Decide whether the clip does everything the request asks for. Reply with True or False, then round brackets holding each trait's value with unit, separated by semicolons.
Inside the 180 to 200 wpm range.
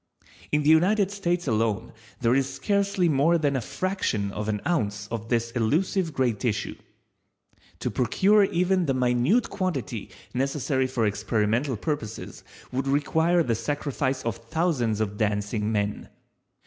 False (140 wpm)